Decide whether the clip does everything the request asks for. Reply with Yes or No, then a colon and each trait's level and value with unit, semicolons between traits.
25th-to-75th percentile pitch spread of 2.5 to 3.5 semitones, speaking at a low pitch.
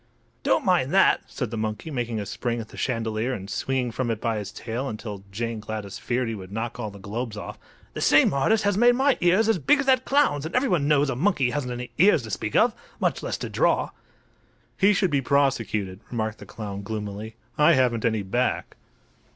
No: wide, 5.4 semitones; low, 120 Hz